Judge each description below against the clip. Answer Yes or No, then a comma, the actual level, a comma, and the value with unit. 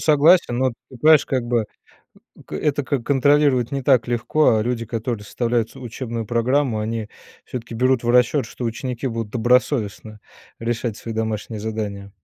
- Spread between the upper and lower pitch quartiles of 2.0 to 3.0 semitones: Yes, average, 2.7 semitones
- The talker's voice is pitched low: Yes, low, 120 Hz